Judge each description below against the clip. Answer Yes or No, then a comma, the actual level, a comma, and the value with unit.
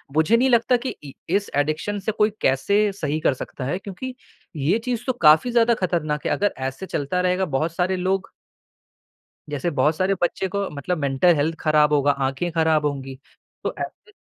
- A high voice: No, medium, 165 Hz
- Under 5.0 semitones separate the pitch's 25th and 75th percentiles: No, wide, 5.5 semitones